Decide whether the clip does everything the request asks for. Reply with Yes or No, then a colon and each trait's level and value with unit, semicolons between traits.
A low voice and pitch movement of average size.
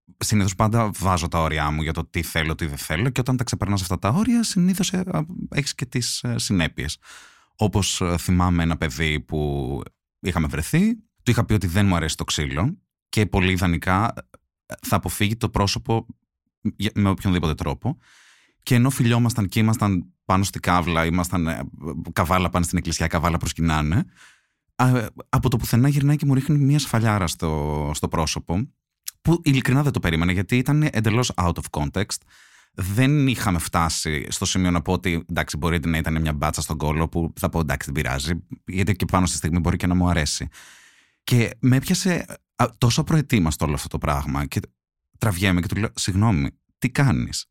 No: very low, 95 Hz; wide, 6.5 semitones